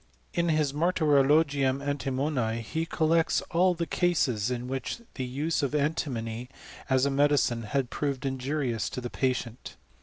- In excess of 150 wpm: No, average, 145 wpm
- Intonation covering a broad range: No, average, 3.5 semitones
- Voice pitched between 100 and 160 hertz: Yes, medium, 140 Hz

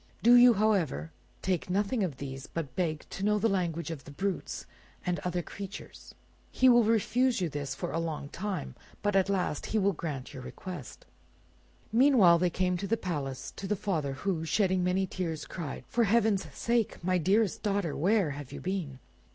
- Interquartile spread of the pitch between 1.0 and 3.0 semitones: No, average, 4.4 semitones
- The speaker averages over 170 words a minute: Yes, average, 185 wpm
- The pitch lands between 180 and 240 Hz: Yes, medium, 185 Hz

